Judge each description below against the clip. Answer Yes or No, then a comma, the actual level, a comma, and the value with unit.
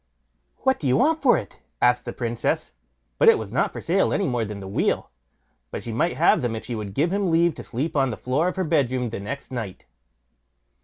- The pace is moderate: No, fast, 225 wpm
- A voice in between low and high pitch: No, low, 130 Hz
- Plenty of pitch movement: Yes, wide, 6.6 semitones